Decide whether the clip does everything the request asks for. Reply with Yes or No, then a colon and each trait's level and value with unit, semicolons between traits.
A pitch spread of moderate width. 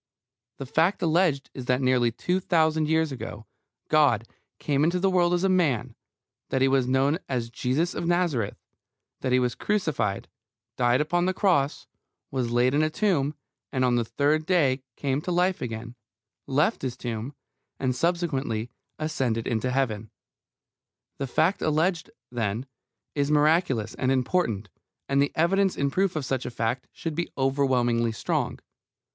Yes: average, 4.9 semitones